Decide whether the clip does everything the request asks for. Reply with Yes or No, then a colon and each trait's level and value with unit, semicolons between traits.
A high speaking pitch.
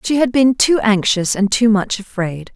Yes: high, 215 Hz